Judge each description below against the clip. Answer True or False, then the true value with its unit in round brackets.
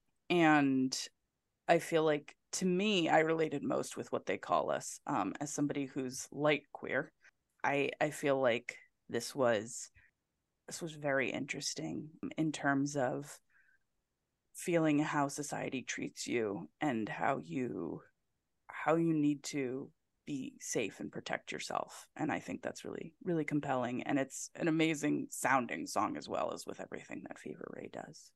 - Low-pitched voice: False (150 Hz)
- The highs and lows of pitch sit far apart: False (2.6 semitones)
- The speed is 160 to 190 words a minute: False (150 wpm)